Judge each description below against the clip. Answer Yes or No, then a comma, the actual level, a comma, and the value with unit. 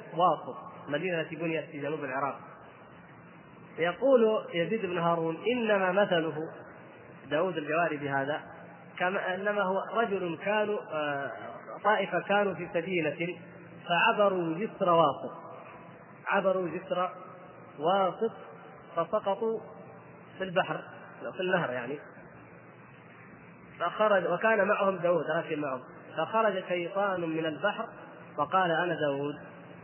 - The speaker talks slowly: No, average, 100 wpm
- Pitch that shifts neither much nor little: Yes, average, 3.3 semitones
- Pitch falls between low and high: Yes, medium, 175 Hz